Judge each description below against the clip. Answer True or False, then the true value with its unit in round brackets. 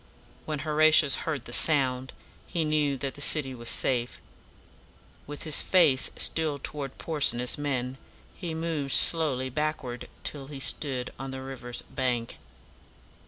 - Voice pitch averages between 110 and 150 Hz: True (140 Hz)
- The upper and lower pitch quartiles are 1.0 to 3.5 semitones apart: True (3.0 semitones)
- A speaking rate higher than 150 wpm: False (140 wpm)